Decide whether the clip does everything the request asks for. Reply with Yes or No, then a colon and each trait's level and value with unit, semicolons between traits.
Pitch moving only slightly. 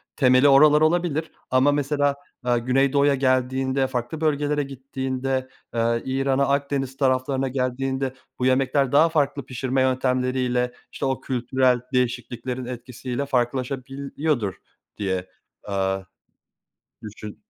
Yes: narrow, 1.8 semitones